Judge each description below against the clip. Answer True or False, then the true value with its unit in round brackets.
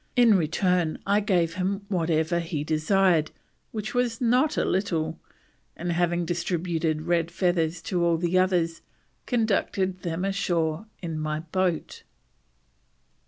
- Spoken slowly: True (125 wpm)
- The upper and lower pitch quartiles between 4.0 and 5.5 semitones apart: False (2.8 semitones)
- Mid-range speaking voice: True (175 Hz)